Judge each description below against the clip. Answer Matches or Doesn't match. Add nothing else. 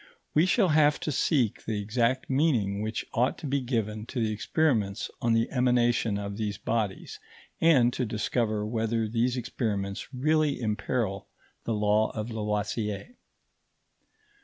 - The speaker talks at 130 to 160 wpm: Matches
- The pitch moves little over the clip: Doesn't match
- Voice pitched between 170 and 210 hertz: Doesn't match